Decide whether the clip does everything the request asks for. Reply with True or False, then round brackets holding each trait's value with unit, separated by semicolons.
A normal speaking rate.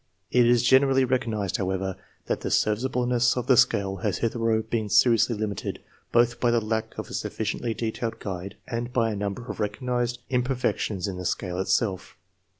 True (170 wpm)